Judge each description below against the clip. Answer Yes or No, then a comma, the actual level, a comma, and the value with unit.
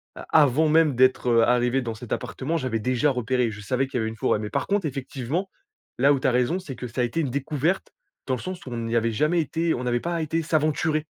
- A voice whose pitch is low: Yes, low, 130 Hz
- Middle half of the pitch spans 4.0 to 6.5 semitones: Yes, average, 4.4 semitones